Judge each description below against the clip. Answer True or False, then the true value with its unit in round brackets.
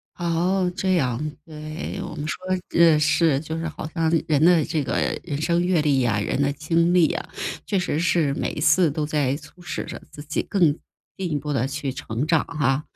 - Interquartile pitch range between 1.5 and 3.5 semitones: True (2.7 semitones)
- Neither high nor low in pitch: True (155 Hz)